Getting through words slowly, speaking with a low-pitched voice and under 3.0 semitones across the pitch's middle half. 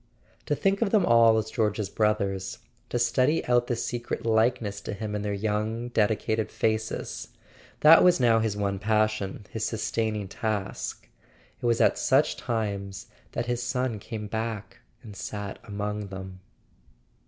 No: average, 155 wpm; low, 110 Hz; narrow, 2.4 semitones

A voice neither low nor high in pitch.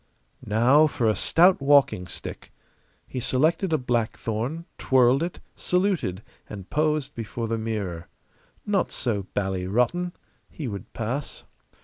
No: low, 125 Hz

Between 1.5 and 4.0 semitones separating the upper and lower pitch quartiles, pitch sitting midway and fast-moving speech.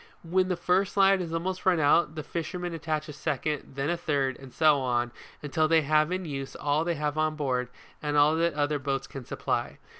Yes: average, 2.9 semitones; medium, 155 Hz; fast, 220 wpm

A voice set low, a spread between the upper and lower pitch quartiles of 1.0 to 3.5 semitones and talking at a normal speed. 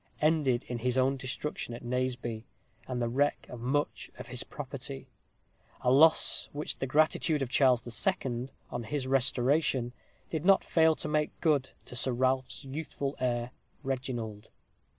Yes: low, 130 Hz; average, 3.0 semitones; average, 150 wpm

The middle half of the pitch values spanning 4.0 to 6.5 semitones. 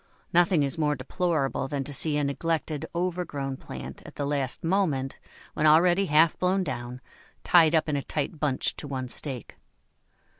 No: average, 3.5 semitones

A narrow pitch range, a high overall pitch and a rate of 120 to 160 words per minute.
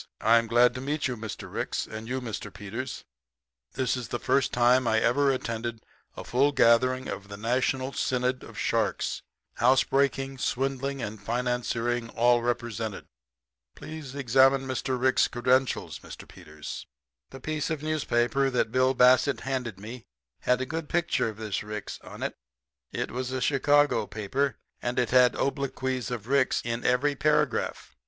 No: narrow, 2.3 semitones; low, 125 Hz; average, 155 wpm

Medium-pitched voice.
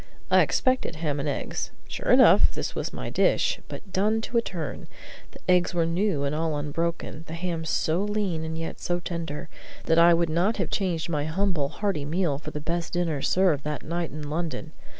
Yes: medium, 165 Hz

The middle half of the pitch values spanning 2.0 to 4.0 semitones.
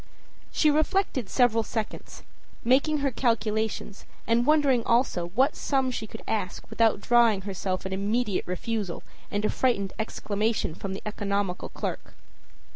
Yes: average, 3.7 semitones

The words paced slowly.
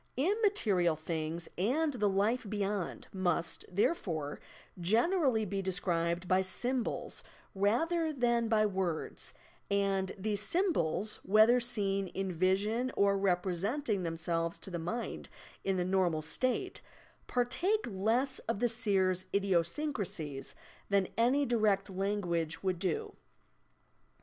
Yes: slow, 115 wpm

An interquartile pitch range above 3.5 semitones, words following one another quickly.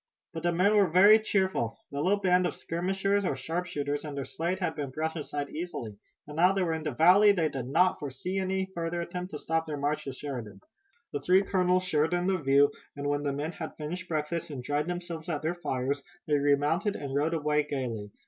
Yes: average, 3.9 semitones; fast, 220 wpm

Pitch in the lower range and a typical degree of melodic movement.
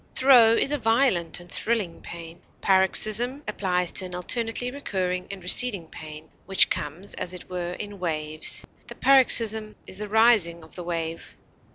No: high, 190 Hz; average, 4.7 semitones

